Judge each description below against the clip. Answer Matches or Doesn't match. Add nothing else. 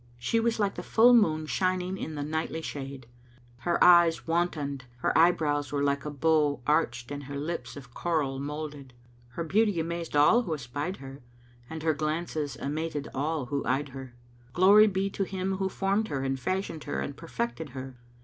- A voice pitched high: Doesn't match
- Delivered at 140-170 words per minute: Doesn't match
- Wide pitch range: Doesn't match